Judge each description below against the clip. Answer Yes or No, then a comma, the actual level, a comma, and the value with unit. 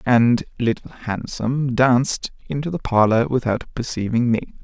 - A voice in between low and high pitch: No, low, 120 Hz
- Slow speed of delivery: Yes, slow, 130 wpm